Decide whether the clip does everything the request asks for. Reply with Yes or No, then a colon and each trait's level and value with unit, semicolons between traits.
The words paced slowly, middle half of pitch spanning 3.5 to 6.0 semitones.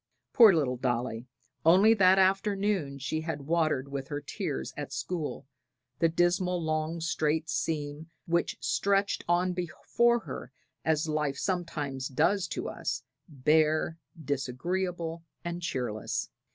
Yes: slow, 125 wpm; average, 3.9 semitones